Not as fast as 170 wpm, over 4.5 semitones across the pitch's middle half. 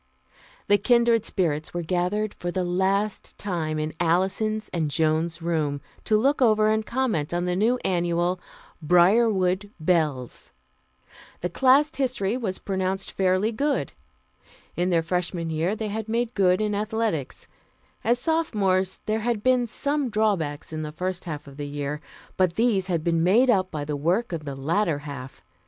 Yes: average, 160 wpm; average, 4.9 semitones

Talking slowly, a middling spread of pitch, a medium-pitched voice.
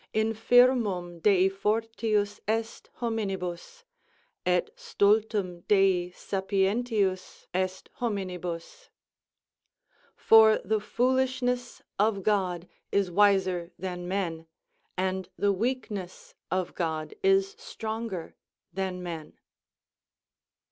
No: slow, 85 wpm; average, 3.6 semitones; high, 200 Hz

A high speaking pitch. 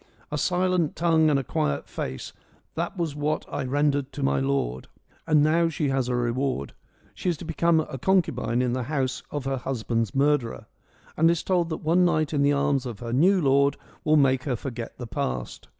No: medium, 140 Hz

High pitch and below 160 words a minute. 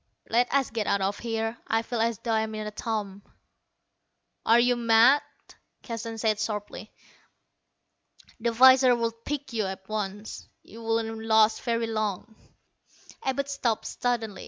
Yes: high, 225 Hz; average, 150 wpm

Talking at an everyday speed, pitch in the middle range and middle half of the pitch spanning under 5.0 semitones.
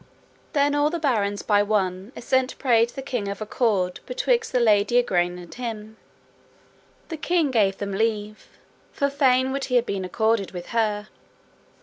No: average, 160 wpm; high, 225 Hz; average, 4.6 semitones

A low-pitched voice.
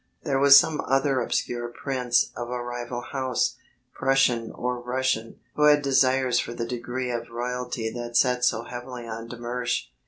Yes: low, 125 Hz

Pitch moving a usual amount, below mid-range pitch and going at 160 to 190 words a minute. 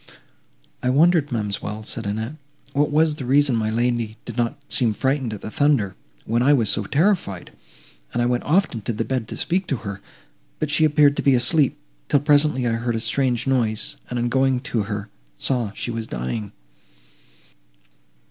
Yes: average, 4.5 semitones; low, 125 Hz; average, 185 wpm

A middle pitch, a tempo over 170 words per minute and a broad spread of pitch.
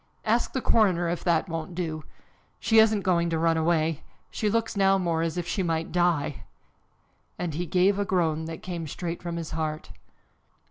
No: medium, 170 Hz; average, 185 wpm; narrow, 2.6 semitones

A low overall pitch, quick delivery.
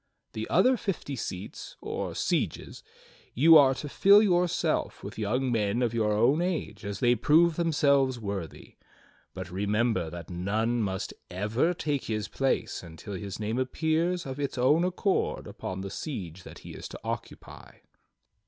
No: low, 120 Hz; average, 155 wpm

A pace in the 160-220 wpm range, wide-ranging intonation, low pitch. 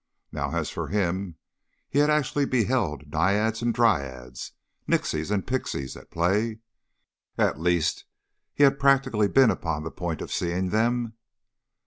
No: average, 140 wpm; wide, 6.4 semitones; low, 105 Hz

